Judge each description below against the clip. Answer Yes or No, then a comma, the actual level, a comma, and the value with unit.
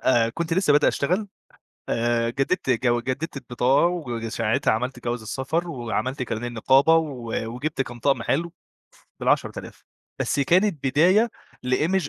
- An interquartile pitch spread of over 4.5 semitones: Yes, wide, 5.4 semitones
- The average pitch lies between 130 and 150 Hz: Yes, low, 135 Hz